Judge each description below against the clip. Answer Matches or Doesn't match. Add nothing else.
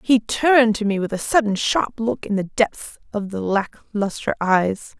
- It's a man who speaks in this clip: Doesn't match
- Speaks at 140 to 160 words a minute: Doesn't match